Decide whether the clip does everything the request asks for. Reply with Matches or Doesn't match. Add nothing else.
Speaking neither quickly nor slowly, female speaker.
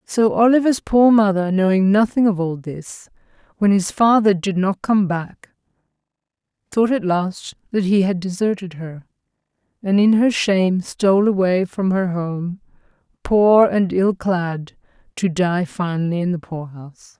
Matches